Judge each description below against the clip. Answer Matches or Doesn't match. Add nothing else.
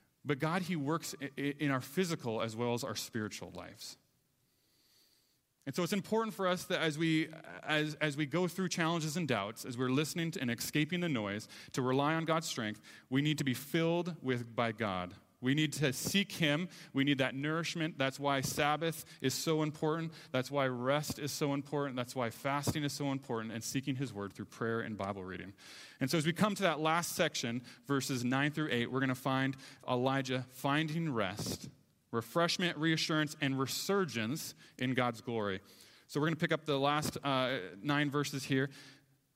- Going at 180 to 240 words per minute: Matches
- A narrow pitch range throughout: Doesn't match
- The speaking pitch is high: Doesn't match